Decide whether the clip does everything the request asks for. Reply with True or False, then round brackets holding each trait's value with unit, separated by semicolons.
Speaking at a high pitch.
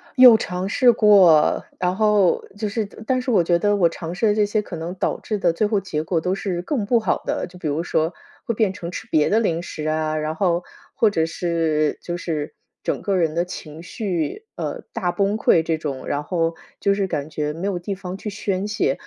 False (180 Hz)